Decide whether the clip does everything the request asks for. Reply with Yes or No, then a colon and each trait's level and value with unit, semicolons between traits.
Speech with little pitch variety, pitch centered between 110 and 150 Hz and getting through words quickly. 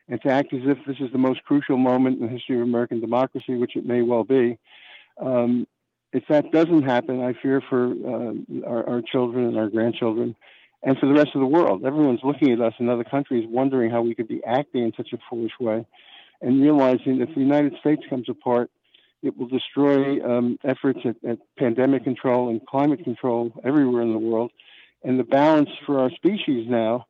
Yes: narrow, 2.3 semitones; low, 125 Hz; fast, 210 wpm